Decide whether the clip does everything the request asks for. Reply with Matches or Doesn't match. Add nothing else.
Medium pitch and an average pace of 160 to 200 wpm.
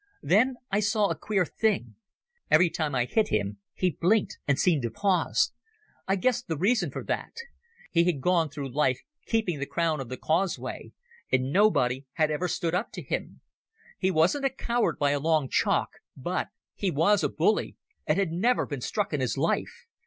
Matches